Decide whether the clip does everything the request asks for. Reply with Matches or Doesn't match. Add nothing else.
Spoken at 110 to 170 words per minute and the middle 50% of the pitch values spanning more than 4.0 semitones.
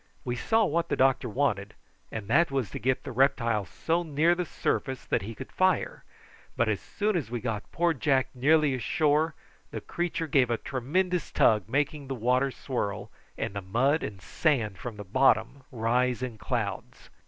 Doesn't match